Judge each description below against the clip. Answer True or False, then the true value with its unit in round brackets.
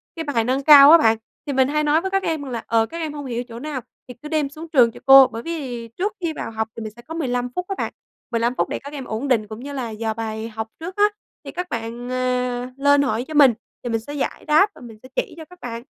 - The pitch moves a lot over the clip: False (4.6 semitones)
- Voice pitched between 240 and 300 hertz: True (260 Hz)